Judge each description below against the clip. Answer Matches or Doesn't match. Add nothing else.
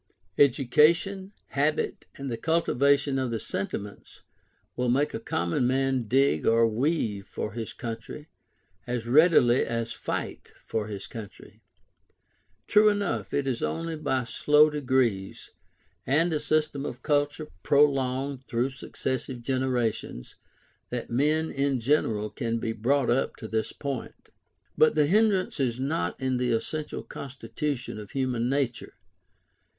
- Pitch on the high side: Doesn't match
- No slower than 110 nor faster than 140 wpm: Matches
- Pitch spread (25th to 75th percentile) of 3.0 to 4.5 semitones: Matches